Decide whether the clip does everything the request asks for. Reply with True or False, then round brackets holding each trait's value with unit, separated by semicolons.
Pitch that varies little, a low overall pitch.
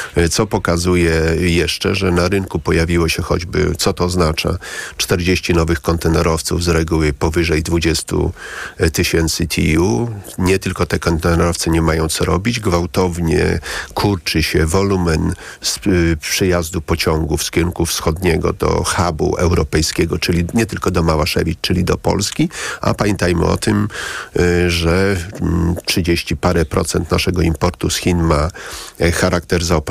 True (1.8 semitones; 85 Hz)